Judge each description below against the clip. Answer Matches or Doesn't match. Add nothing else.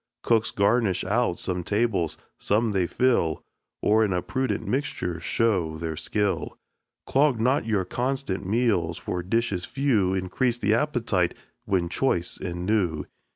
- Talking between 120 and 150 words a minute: Matches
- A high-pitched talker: Doesn't match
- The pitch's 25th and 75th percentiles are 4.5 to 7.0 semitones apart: Matches